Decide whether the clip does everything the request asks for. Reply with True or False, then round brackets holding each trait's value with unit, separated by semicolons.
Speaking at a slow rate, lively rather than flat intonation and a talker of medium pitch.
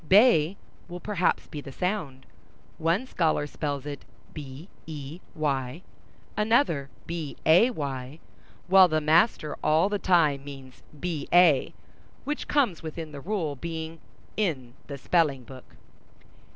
False (110 wpm; 4.3 semitones; 160 Hz)